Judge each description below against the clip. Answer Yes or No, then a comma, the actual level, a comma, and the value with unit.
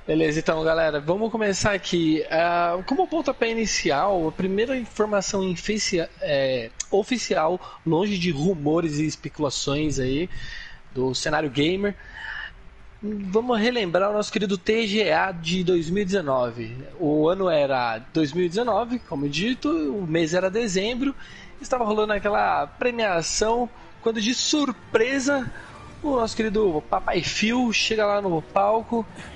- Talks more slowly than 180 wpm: Yes, slow, 120 wpm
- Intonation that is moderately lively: No, wide, 5.9 semitones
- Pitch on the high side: Yes, high, 200 Hz